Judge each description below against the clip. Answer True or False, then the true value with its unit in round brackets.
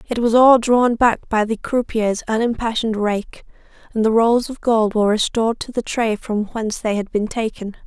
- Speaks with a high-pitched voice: True (225 Hz)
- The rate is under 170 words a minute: False (200 wpm)